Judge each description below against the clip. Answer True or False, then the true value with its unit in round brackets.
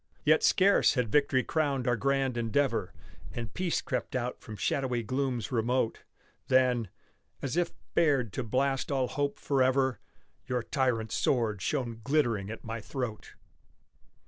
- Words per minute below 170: True (140 wpm)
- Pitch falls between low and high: False (130 Hz)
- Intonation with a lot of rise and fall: False (3.1 semitones)